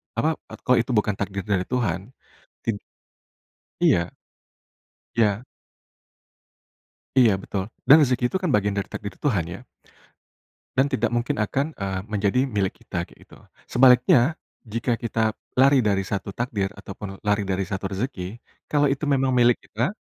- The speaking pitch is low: Yes, low, 110 Hz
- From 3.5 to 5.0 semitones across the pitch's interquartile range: Yes, average, 4.5 semitones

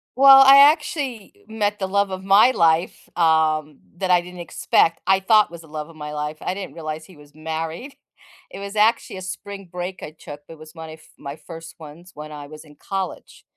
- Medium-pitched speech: Yes, medium, 170 Hz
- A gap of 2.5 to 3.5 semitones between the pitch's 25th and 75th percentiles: No, average, 4.2 semitones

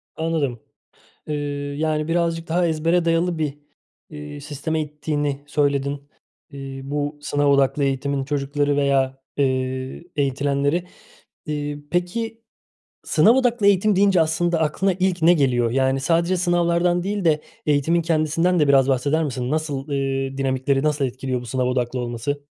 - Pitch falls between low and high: Yes, medium, 145 Hz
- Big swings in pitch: No, average, 3.6 semitones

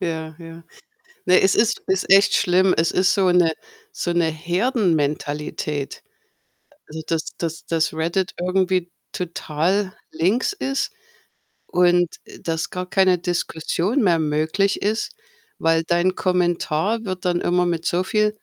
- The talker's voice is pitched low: No, medium, 175 Hz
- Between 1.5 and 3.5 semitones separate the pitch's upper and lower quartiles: Yes, narrow, 2.6 semitones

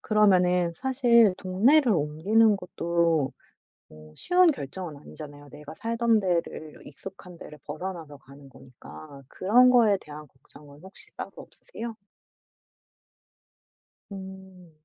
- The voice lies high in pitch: No, medium, 180 Hz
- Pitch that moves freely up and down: Yes, wide, 6.2 semitones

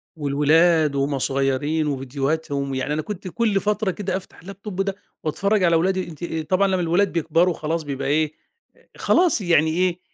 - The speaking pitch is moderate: Yes, medium, 165 Hz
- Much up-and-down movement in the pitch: No, average, 4.3 semitones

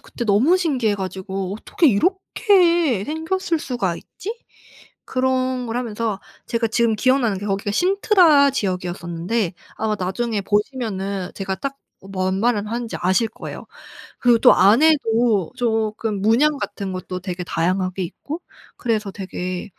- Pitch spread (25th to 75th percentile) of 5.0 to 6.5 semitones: Yes, average, 5.3 semitones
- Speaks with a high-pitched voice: Yes, high, 220 Hz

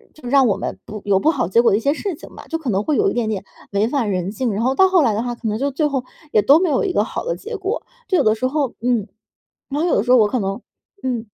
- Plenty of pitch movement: Yes, wide, 5.9 semitones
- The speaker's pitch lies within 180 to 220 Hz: No, very high, 250 Hz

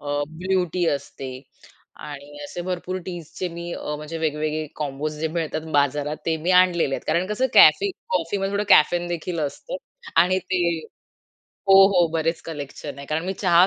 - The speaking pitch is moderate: Yes, medium, 165 Hz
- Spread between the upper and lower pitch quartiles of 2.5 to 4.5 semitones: Yes, average, 3.3 semitones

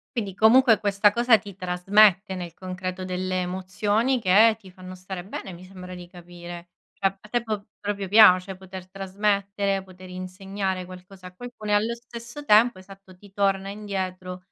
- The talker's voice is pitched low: No, high, 195 Hz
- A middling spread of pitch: No, narrow, 2.1 semitones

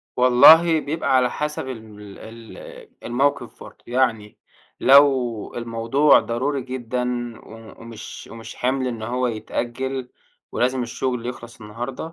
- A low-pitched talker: Yes, low, 125 Hz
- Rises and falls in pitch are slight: Yes, narrow, 2.3 semitones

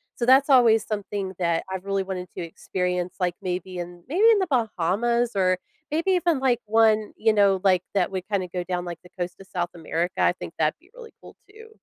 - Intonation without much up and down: No, average, 5.0 semitones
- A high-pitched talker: Yes, high, 195 Hz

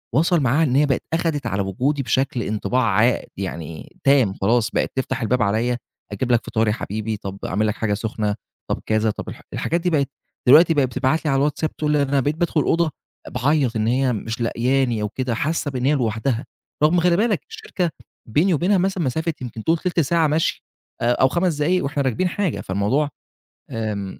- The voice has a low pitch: Yes, low, 130 Hz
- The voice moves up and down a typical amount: No, wide, 5.9 semitones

